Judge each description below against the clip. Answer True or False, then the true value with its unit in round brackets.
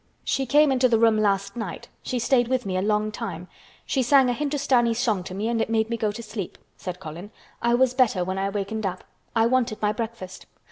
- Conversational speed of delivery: False (230 wpm)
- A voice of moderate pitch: False (225 Hz)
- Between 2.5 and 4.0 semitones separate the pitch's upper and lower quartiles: True (3.7 semitones)